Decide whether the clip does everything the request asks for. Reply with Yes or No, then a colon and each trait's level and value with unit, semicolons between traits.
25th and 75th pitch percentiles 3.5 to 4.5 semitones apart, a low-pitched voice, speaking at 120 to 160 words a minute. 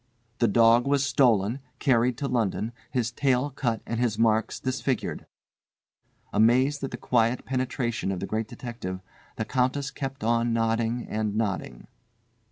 No: narrow, 2.5 semitones; low, 120 Hz; average, 145 wpm